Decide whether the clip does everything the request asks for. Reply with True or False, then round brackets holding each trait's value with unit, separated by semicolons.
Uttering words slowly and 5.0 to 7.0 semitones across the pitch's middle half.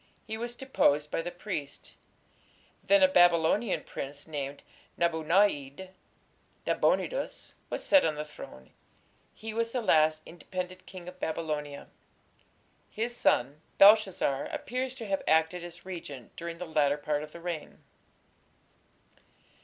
True (130 wpm; 5.3 semitones)